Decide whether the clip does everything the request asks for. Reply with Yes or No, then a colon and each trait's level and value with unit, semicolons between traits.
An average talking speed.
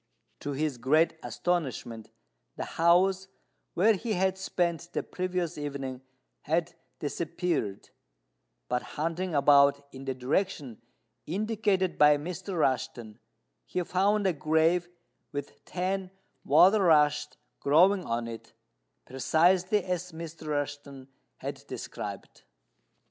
No: slow, 110 wpm